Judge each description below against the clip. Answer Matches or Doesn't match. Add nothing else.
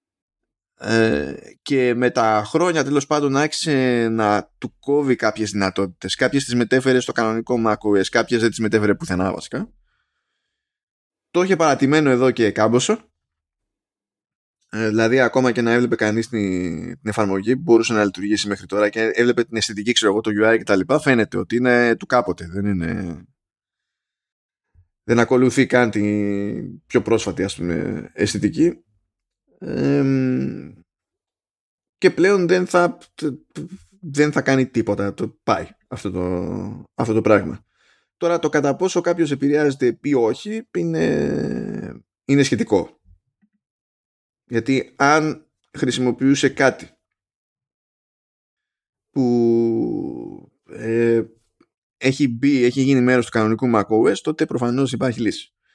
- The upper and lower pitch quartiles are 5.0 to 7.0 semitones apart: Doesn't match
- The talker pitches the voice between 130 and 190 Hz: Doesn't match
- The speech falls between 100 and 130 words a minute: Matches